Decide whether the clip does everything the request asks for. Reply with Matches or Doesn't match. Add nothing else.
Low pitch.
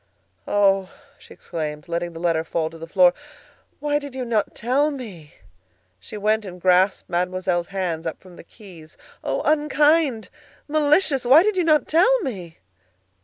Doesn't match